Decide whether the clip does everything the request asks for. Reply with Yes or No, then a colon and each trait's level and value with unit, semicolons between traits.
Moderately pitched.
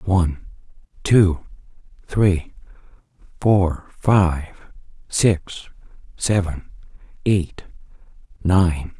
No: very low, 90 Hz